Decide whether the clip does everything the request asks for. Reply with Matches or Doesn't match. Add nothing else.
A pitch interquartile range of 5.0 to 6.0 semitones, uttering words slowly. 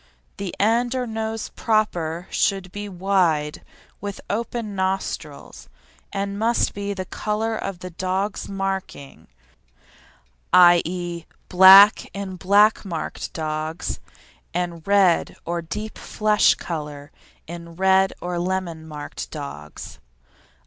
Doesn't match